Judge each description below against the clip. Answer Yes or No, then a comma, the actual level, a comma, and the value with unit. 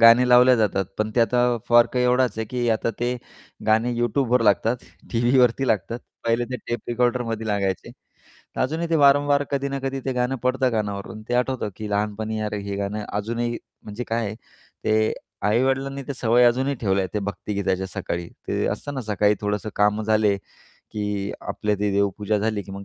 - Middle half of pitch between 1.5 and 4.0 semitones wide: Yes, average, 3.2 semitones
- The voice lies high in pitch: No, low, 115 Hz